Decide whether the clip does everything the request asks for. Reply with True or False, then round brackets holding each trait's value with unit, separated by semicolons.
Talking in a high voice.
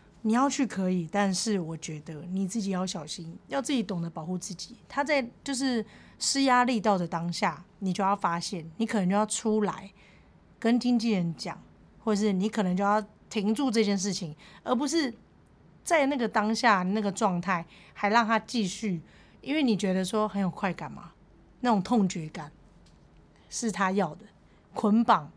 True (205 Hz)